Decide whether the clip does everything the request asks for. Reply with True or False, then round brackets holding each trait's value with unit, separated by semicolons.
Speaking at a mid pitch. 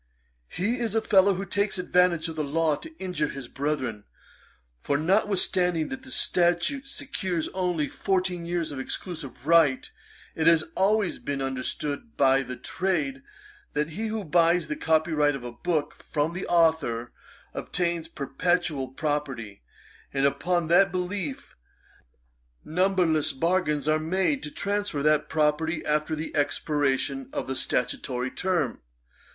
True (160 Hz)